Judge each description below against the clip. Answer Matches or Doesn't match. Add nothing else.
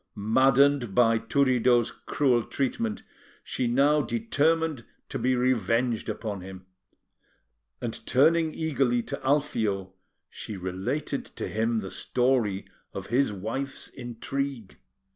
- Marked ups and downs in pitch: Doesn't match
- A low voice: Matches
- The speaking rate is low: Matches